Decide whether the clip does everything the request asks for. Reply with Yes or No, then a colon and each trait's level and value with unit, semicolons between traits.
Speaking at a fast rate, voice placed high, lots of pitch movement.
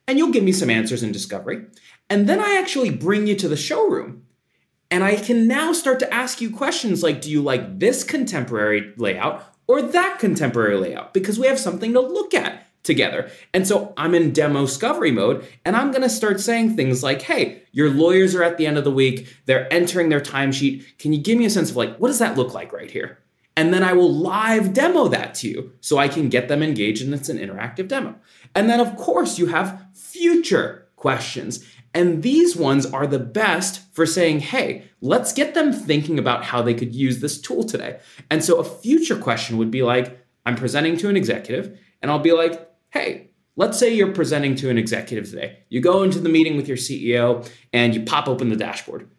No: fast, 215 wpm; medium, 165 Hz; wide, 8.6 semitones